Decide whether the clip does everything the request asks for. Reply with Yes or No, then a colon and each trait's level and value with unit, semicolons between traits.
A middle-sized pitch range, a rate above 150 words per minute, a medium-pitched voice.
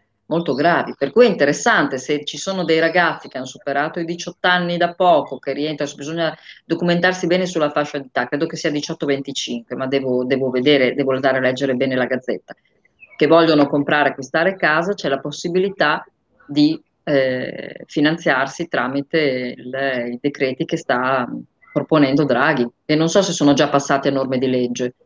Yes: average, 3.4 semitones; fast, 170 wpm; medium, 145 Hz